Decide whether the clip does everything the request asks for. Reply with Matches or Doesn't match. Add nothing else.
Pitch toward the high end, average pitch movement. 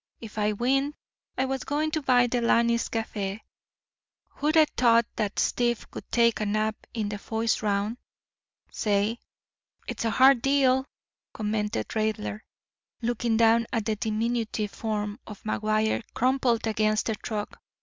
Doesn't match